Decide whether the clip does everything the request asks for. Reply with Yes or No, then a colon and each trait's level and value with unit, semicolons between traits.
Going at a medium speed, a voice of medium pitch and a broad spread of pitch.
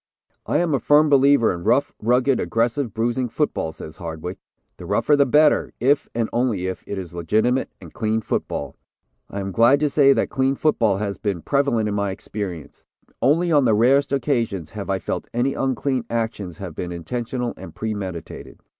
No: average, 180 wpm; low, 115 Hz; wide, 5.8 semitones